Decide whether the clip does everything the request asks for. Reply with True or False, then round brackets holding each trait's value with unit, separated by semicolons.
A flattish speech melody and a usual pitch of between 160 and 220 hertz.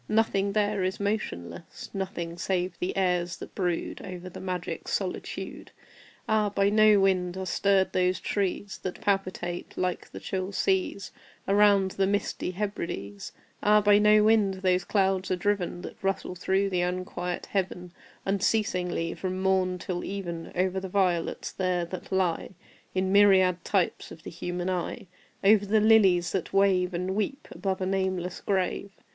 True (1.8 semitones; 190 Hz)